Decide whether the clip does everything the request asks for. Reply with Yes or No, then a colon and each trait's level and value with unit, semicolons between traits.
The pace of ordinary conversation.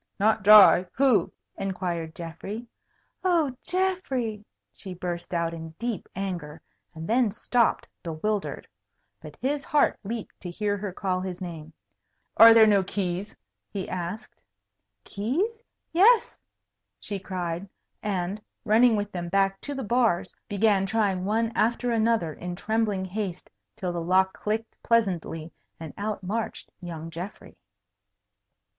No: slow, 130 wpm